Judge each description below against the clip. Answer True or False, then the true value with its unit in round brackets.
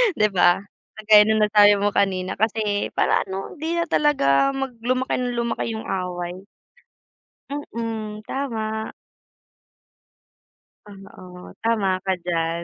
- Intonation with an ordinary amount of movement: True (3.6 semitones)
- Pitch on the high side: True (210 Hz)